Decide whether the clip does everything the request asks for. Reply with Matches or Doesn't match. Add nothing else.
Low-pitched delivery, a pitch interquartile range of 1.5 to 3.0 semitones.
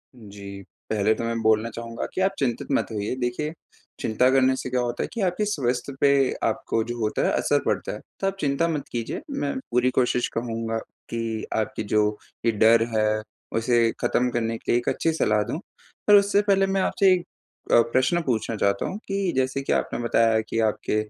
Doesn't match